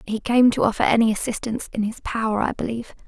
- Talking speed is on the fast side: Yes, fast, 215 wpm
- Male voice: No, female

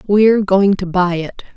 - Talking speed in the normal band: Yes, average, 190 wpm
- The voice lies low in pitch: No, high, 190 Hz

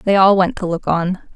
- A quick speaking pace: Yes, fast, 265 wpm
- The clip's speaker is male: No, female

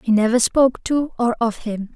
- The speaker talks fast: Yes, fast, 215 wpm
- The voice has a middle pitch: No, high, 235 Hz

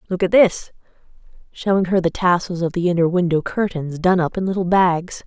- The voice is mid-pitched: Yes, medium, 180 Hz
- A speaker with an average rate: Yes, average, 195 wpm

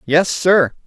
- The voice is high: No, medium, 165 Hz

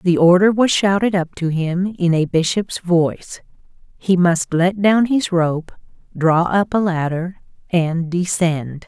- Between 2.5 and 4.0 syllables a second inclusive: Yes, 3.8 syllables/s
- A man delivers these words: No, female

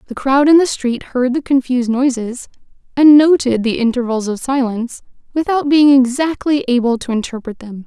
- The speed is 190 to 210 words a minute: No, average, 170 wpm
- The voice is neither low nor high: No, very high, 260 Hz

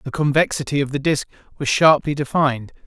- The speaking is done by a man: Yes, male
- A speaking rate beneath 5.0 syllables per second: No, 6.0 syllables/s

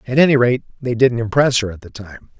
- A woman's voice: No, male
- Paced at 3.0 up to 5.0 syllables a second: No, 6.0 syllables/s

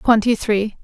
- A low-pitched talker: No, high, 220 Hz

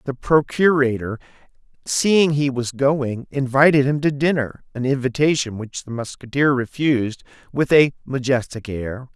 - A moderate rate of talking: No, slow, 125 wpm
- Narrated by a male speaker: Yes, male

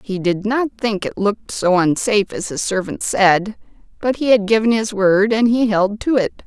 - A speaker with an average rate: No, fast, 215 wpm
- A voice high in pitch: Yes, high, 210 Hz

